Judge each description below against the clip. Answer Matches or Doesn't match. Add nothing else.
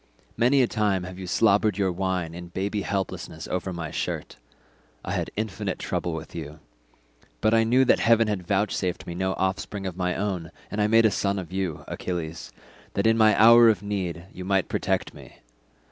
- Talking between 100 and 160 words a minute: Doesn't match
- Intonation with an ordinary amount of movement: Matches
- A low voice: Matches